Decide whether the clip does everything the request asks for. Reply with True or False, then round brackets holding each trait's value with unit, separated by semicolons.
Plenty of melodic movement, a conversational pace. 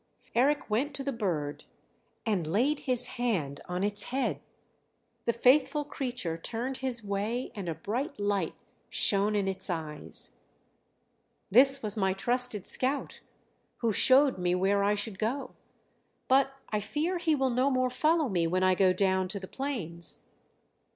True (5.7 semitones; 155 wpm)